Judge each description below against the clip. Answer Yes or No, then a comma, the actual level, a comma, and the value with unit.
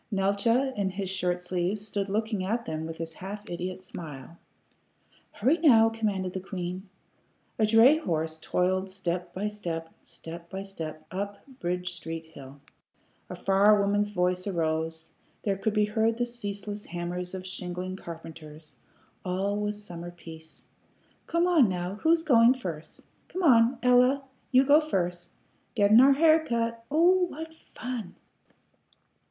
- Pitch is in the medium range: No, high, 195 Hz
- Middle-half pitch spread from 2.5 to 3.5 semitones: No, average, 4.5 semitones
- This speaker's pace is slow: No, average, 145 wpm